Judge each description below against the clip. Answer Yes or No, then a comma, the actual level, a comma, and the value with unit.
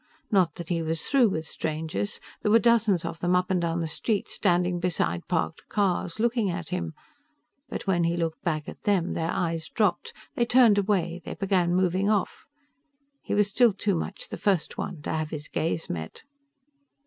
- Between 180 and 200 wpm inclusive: Yes, average, 190 wpm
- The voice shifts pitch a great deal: No, average, 3.8 semitones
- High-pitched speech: No, medium, 180 Hz